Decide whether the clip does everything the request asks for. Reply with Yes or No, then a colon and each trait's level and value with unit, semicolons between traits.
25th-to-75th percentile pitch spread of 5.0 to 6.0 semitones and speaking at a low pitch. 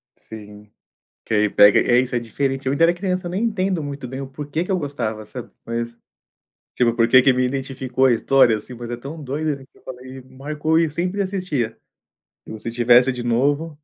No: average, 4.2 semitones; low, 130 Hz